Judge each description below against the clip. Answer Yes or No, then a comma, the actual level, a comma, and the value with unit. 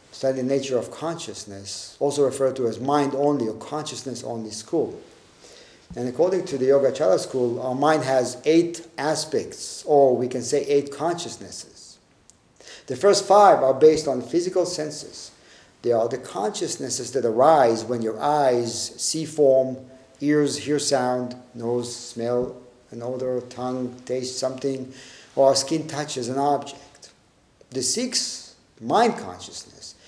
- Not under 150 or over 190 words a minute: No, average, 140 wpm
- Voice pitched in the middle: No, low, 130 Hz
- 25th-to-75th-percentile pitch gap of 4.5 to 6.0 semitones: No, average, 2.9 semitones